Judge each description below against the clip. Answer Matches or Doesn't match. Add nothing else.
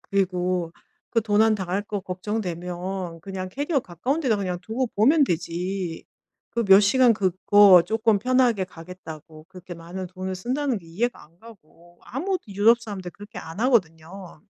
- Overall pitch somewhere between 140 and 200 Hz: Matches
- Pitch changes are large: Doesn't match